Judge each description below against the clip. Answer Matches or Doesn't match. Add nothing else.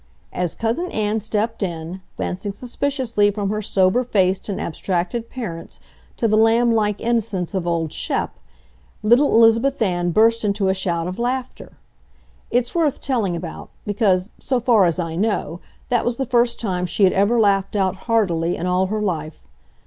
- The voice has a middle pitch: Doesn't match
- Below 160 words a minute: Doesn't match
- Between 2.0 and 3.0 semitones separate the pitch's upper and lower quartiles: Doesn't match